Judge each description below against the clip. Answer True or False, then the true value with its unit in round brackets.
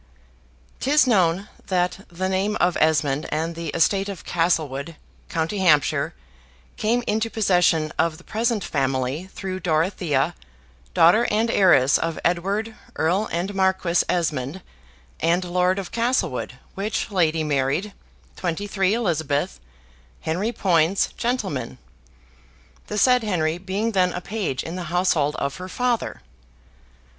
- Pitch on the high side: False (180 Hz)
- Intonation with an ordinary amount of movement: True (4.1 semitones)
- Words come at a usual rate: False (125 wpm)